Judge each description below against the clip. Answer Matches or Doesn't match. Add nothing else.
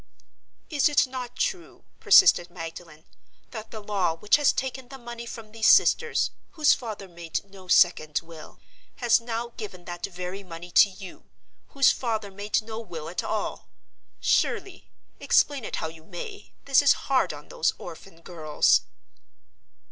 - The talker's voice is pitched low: Doesn't match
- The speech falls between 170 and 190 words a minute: Doesn't match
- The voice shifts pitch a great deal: Matches